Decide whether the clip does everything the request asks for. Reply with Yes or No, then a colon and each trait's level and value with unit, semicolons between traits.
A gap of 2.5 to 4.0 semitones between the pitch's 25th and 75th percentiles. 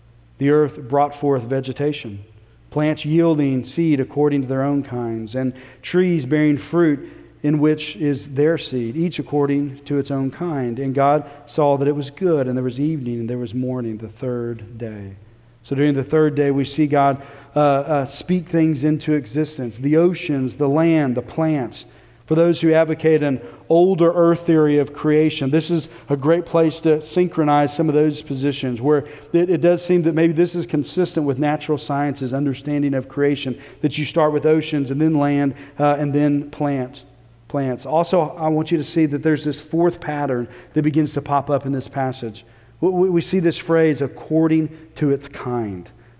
Yes: average, 2.8 semitones